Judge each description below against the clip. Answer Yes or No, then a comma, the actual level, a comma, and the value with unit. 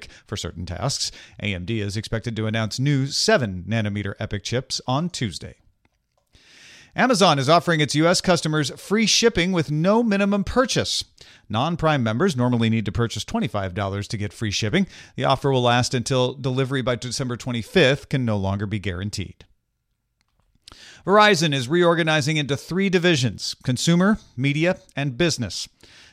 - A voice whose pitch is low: Yes, low, 130 Hz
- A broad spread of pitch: Yes, wide, 7.3 semitones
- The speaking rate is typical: Yes, average, 145 wpm